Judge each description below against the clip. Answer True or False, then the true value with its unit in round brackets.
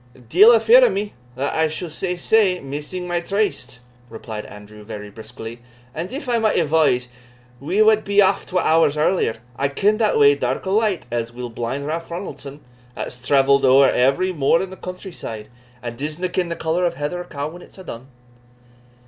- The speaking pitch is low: False (160 Hz)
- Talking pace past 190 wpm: True (200 wpm)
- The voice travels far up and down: True (6.2 semitones)